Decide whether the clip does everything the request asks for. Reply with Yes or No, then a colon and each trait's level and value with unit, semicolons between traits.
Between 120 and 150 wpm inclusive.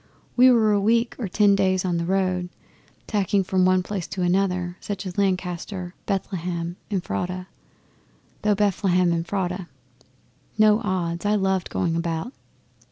Yes: average, 145 wpm